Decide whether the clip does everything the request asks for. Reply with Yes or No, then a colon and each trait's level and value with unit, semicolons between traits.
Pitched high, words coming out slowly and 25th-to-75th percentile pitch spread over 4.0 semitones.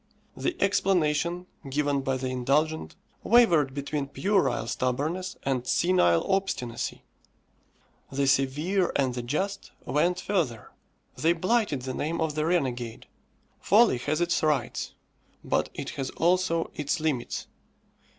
No: medium, 150 Hz; slow, 120 wpm; average, 5.2 semitones